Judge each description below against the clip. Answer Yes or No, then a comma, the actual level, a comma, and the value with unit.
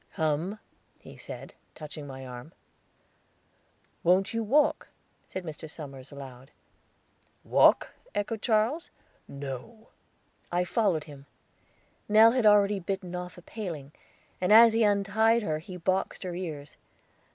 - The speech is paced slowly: Yes, slow, 125 wpm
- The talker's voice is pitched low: No, medium, 180 Hz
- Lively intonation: Yes, wide, 6.1 semitones